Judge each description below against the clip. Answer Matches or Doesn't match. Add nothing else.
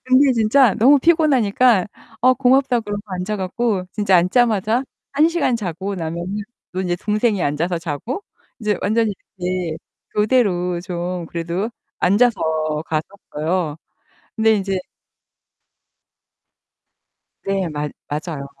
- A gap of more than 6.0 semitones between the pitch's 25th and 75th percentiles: Doesn't match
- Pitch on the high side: Matches